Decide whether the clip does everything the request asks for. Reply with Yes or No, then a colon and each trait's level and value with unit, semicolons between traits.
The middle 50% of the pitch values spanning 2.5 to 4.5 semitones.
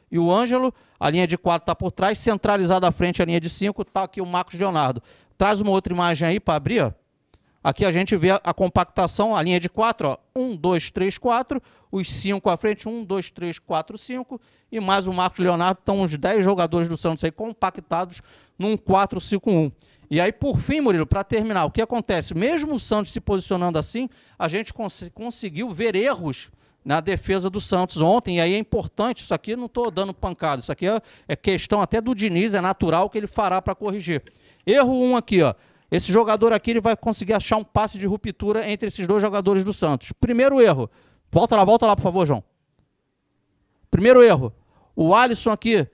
Yes: average, 3.7 semitones